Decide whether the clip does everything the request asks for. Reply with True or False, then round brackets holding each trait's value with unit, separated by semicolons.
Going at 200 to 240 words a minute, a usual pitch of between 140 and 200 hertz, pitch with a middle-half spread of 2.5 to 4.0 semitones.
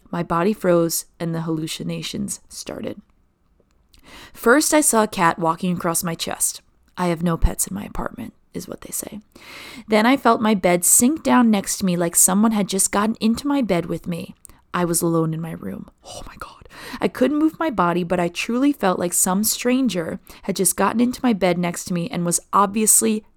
False (205 wpm; 190 Hz; 4.7 semitones)